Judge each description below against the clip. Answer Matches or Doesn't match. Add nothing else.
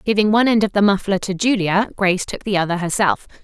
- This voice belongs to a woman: Matches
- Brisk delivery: Matches